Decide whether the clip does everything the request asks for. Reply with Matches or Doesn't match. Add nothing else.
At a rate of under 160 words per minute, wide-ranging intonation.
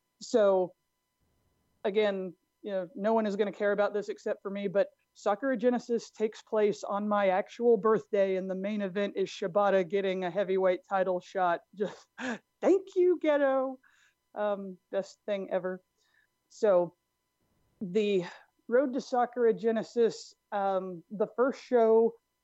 Doesn't match